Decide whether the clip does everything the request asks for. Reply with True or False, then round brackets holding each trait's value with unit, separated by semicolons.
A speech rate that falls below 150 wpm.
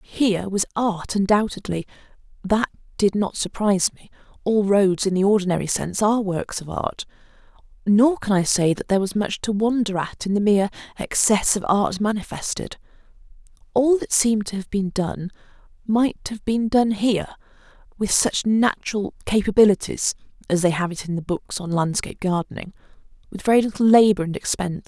False (155 wpm)